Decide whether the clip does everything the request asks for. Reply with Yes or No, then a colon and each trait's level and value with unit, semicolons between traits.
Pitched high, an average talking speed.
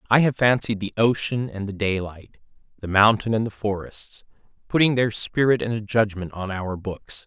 No: low, 105 Hz; average, 180 wpm